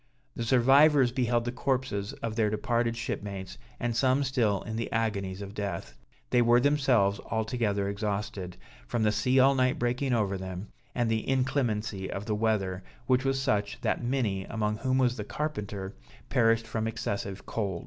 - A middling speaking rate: Yes, average, 170 wpm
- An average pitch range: Yes, average, 3.7 semitones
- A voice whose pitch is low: Yes, low, 115 Hz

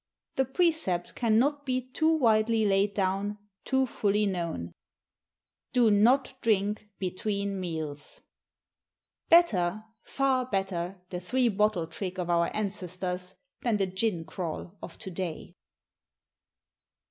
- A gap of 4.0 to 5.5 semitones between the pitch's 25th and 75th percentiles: Yes, average, 4.5 semitones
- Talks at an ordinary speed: No, slow, 115 wpm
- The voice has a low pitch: No, high, 200 Hz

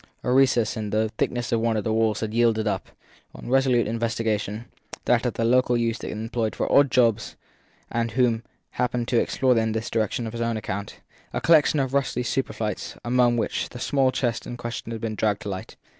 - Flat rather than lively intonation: Yes, narrow, 2.0 semitones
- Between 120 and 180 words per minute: No, fast, 205 wpm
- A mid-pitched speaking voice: No, low, 115 Hz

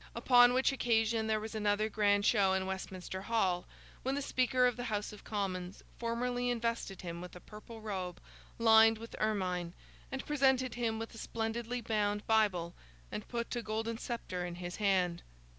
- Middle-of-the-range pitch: No, high, 220 Hz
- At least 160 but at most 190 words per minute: Yes, average, 175 wpm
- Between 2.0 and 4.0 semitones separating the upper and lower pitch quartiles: Yes, average, 3.6 semitones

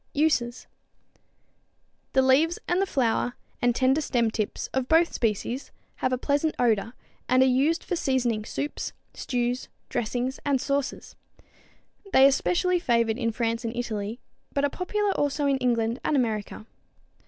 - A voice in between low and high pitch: No, very high, 255 Hz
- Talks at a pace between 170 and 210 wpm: No, average, 150 wpm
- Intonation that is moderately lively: Yes, average, 3.4 semitones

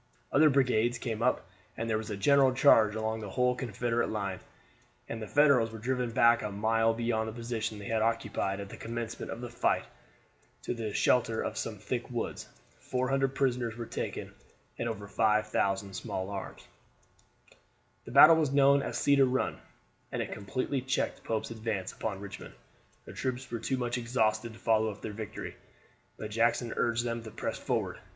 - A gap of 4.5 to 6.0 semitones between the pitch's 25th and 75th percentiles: No, narrow, 2.5 semitones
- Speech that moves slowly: No, average, 180 wpm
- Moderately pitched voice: No, low, 115 Hz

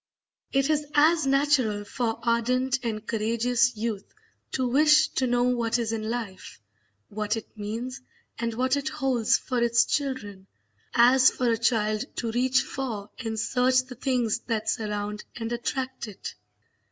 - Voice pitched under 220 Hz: No, high, 235 Hz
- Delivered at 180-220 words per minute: No, average, 155 wpm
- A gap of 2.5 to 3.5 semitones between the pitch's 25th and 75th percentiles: Yes, average, 2.9 semitones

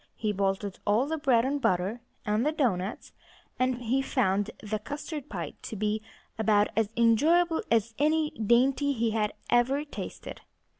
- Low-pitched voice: No, high, 230 Hz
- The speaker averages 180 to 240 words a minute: No, average, 155 wpm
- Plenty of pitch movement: No, average, 4.9 semitones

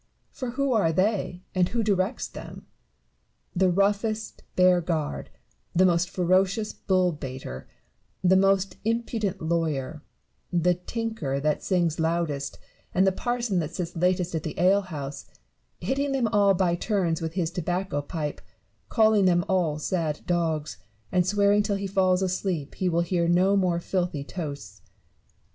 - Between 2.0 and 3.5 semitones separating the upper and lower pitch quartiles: Yes, average, 3.2 semitones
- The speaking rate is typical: Yes, average, 155 wpm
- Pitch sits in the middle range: Yes, medium, 180 Hz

